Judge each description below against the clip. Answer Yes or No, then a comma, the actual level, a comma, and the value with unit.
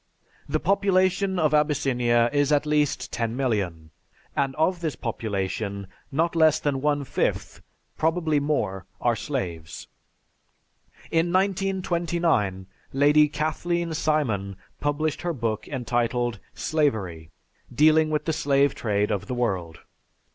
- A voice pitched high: No, medium, 145 Hz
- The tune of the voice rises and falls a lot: Yes, wide, 5.9 semitones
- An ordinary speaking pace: No, slow, 120 wpm